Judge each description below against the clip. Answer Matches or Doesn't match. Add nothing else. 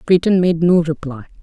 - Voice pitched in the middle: Matches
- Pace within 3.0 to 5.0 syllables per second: Doesn't match